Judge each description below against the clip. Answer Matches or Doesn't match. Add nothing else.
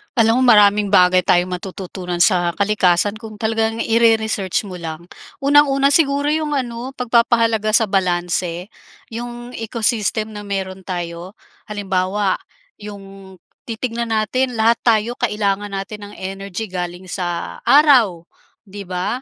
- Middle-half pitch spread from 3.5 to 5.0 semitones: Matches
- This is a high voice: Matches